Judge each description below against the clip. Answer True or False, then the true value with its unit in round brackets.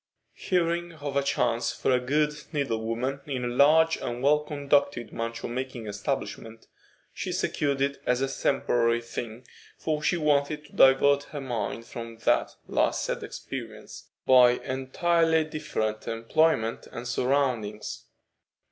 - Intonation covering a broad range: False (4.1 semitones)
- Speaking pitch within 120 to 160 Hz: True (135 Hz)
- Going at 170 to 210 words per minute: False (140 wpm)